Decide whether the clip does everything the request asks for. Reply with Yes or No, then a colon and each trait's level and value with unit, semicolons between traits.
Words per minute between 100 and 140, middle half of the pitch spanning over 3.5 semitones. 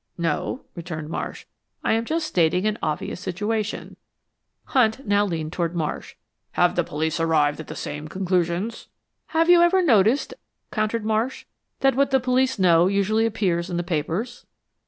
No: average, 155 wpm; wide, 5.5 semitones